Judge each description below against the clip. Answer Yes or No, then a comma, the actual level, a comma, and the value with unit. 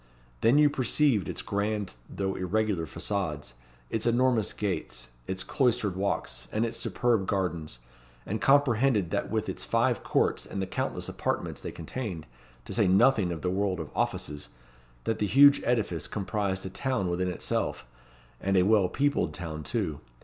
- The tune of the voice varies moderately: Yes, average, 4.5 semitones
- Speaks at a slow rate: No, average, 160 wpm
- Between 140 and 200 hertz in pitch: No, low, 100 Hz